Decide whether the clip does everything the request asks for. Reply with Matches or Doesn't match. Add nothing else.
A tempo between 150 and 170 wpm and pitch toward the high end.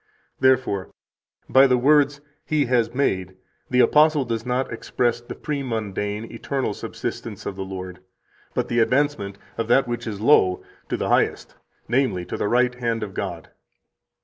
Doesn't match